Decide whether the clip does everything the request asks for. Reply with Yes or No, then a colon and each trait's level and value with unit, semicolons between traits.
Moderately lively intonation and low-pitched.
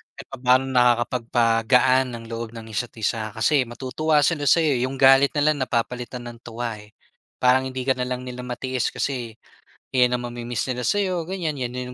No: narrow, 2.0 semitones; low, 125 Hz